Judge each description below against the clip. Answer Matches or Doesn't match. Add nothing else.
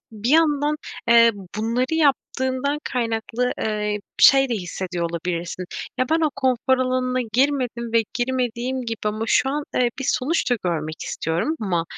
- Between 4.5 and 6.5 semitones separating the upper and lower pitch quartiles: Doesn't match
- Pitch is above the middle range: Matches